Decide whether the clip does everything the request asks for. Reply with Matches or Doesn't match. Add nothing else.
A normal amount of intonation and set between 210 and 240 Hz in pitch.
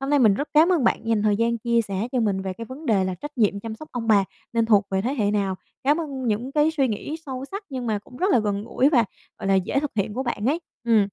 Matches